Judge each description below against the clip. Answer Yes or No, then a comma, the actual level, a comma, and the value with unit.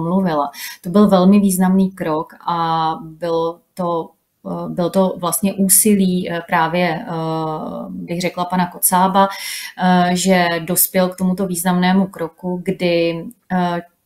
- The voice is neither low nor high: Yes, medium, 180 Hz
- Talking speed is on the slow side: Yes, slow, 105 wpm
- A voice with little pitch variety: Yes, narrow, 1.9 semitones